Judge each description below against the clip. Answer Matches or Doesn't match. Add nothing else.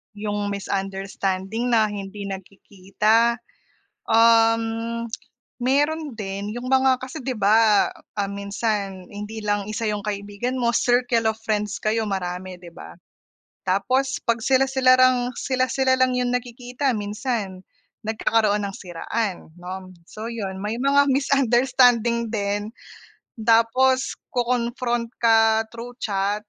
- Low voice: Doesn't match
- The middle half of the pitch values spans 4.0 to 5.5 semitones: Doesn't match